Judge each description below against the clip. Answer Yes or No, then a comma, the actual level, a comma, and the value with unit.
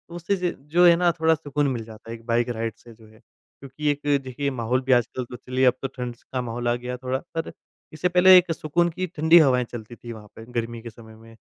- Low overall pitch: Yes, low, 130 Hz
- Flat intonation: No, average, 5.0 semitones